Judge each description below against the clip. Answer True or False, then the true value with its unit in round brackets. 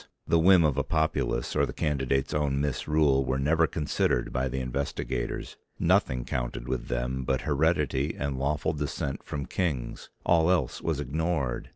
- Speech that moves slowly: False (160 wpm)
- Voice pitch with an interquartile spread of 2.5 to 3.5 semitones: True (3.2 semitones)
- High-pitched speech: False (70 Hz)